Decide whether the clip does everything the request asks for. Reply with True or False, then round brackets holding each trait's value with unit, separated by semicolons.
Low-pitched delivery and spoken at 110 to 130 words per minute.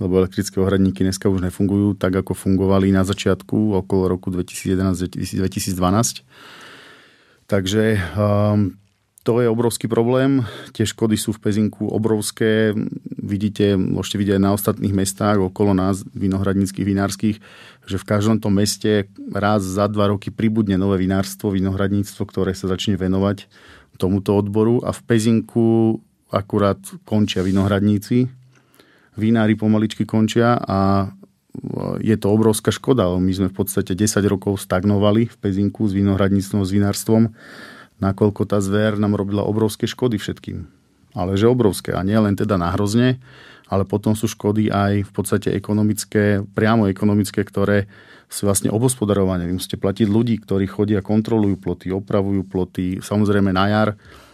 False (100 Hz; 140 wpm)